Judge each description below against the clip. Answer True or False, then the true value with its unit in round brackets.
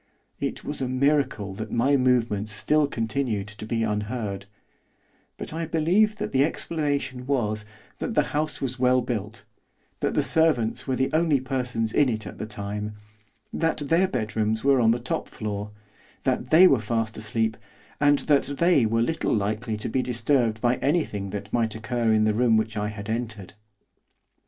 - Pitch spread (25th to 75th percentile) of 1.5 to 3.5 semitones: False (4.3 semitones)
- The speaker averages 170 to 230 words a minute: True (175 wpm)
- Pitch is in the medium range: False (120 Hz)